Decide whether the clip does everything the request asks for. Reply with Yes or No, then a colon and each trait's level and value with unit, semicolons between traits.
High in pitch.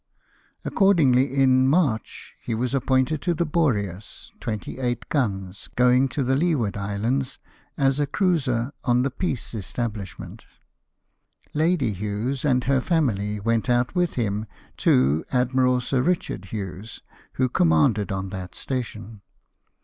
No: low, 125 Hz